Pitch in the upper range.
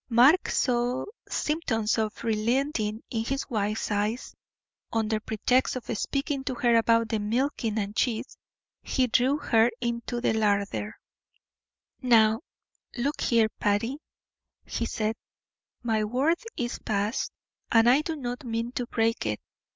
Yes: high, 230 Hz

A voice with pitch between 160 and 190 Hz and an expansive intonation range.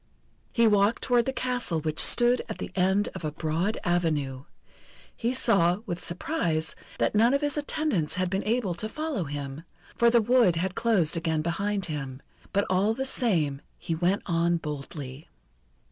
Yes: medium, 185 Hz; wide, 6.4 semitones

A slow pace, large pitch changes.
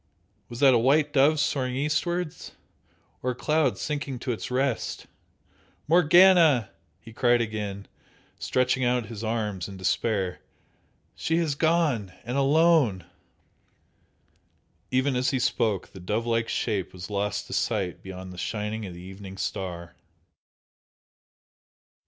Yes: slow, 130 wpm; wide, 5.9 semitones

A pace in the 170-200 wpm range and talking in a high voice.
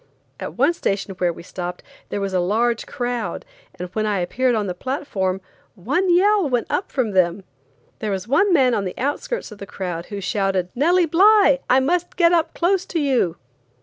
Yes: average, 195 wpm; high, 240 Hz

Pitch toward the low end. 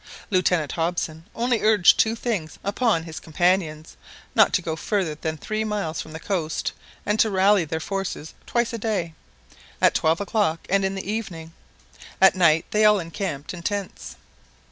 No: medium, 185 Hz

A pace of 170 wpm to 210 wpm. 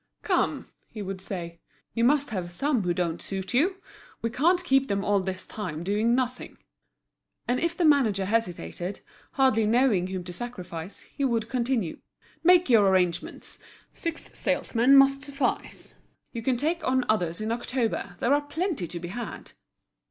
No: average, 160 wpm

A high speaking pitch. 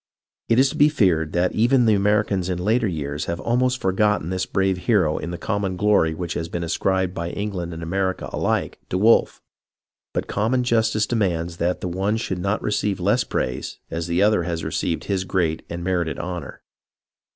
No: very low, 95 Hz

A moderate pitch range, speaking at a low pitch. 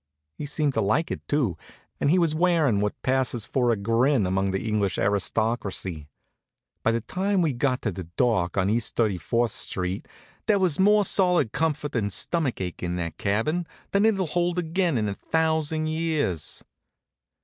No: wide, 8.2 semitones; low, 125 Hz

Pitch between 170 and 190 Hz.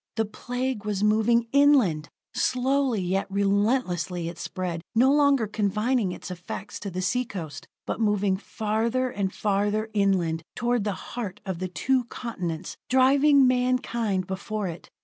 No: high, 210 Hz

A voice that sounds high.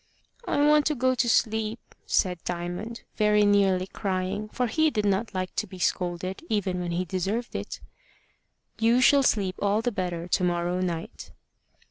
Yes: high, 200 Hz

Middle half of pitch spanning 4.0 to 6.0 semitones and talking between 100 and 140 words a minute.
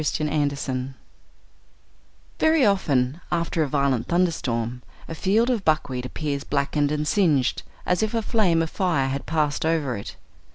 No: average, 4.4 semitones; average, 155 wpm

